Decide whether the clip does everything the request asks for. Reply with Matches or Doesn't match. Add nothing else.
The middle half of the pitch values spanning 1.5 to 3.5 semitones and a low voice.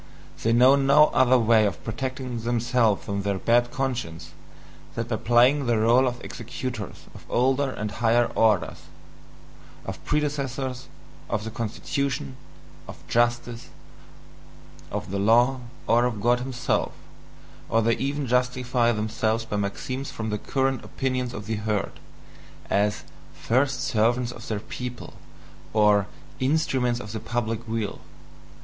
Matches